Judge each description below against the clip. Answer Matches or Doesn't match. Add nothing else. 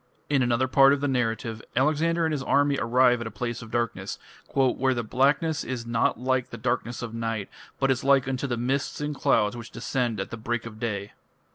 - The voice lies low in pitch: Matches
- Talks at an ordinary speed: Doesn't match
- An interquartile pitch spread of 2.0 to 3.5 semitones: Matches